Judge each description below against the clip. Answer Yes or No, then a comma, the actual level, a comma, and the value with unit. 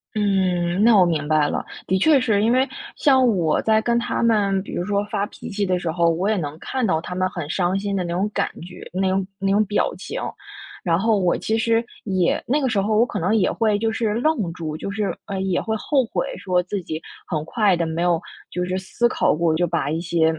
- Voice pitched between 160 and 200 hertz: Yes, high, 195 Hz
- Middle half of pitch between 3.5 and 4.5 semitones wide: Yes, average, 4.0 semitones